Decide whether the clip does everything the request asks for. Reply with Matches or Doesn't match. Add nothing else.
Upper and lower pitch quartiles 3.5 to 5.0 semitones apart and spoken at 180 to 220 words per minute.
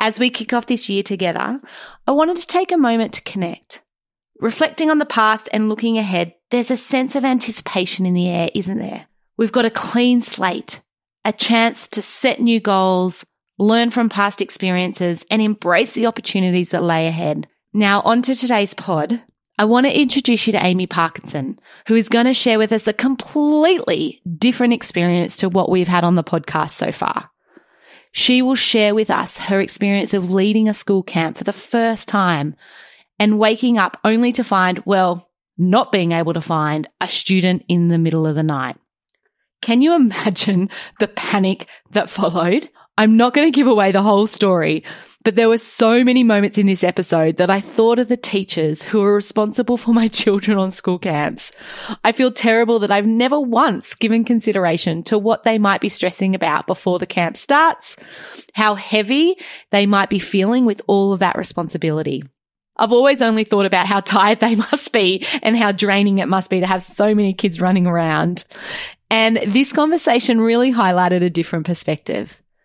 Matches